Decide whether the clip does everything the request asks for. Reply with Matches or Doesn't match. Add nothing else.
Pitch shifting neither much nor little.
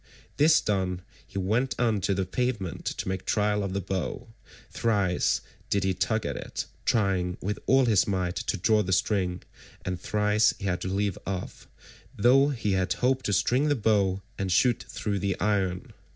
Matches